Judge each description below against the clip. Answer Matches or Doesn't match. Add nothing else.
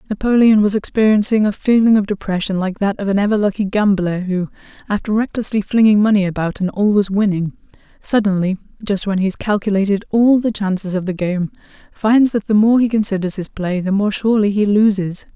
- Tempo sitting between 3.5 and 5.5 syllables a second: Doesn't match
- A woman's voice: Matches